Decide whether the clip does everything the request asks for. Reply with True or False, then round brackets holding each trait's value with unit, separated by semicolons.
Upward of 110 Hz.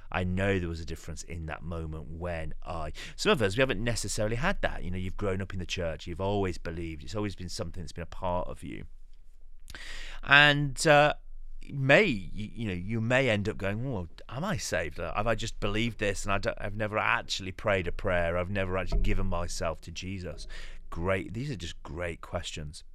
False (95 Hz)